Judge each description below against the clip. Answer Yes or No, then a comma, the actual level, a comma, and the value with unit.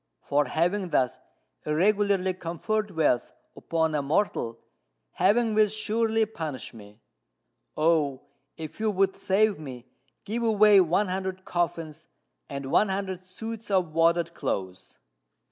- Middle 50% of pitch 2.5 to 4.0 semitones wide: No, average, 5.1 semitones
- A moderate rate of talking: No, slow, 125 wpm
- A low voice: No, medium, 180 Hz